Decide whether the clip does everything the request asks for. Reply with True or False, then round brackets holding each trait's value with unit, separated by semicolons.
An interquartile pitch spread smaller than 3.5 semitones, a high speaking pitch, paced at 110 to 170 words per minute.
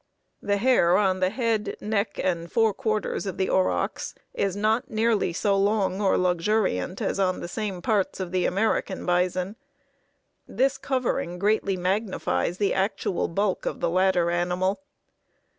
True (2.8 semitones; 195 Hz; 145 wpm)